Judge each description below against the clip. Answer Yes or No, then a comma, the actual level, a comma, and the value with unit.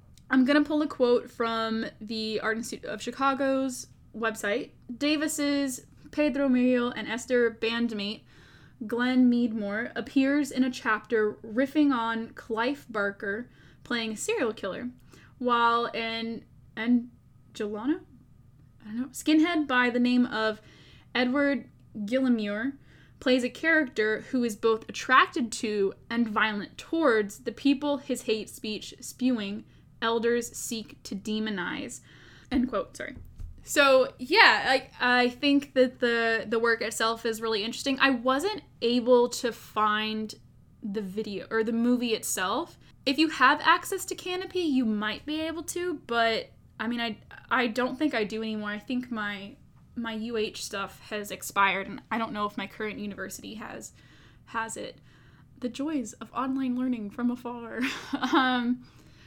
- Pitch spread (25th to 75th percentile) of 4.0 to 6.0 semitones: No, average, 3.2 semitones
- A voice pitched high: Yes, high, 240 Hz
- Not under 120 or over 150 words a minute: Yes, average, 145 wpm